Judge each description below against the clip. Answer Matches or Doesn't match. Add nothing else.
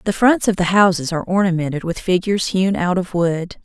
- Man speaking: Doesn't match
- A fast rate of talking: Matches